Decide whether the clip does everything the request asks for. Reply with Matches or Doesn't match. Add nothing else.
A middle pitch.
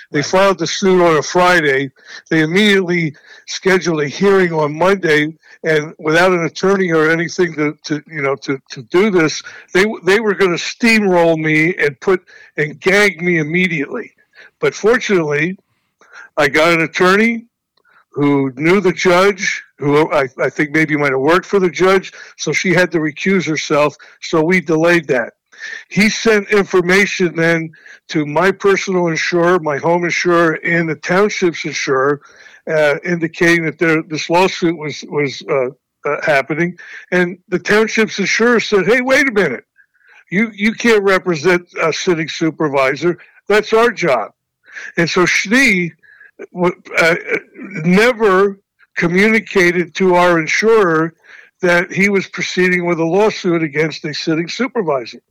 Matches